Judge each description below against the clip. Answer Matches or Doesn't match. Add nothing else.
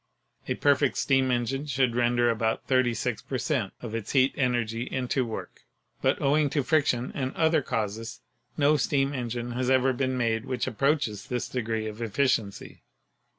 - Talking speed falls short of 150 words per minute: Doesn't match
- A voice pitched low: Matches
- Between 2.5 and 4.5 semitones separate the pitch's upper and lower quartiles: Matches